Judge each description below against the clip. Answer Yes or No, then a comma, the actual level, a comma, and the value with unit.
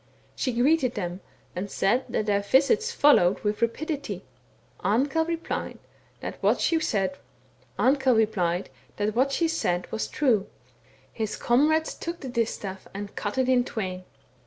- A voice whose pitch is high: Yes, high, 235 Hz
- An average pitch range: No, wide, 5.9 semitones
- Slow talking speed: Yes, slow, 120 wpm